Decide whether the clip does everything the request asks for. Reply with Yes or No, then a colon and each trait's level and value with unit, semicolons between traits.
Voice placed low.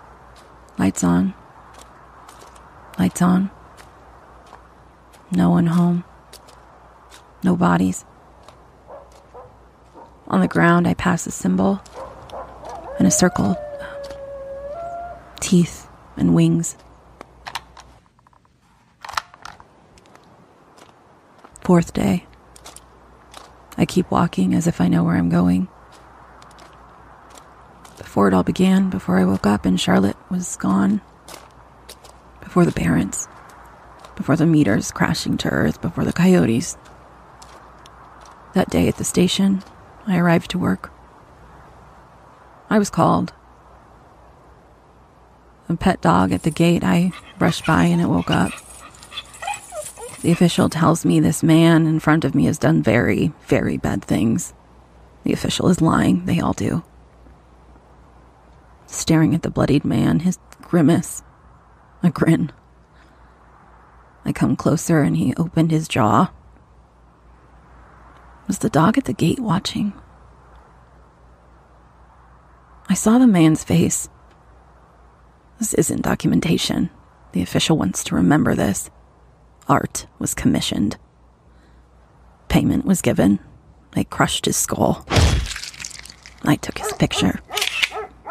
Yes: very low, 95 Hz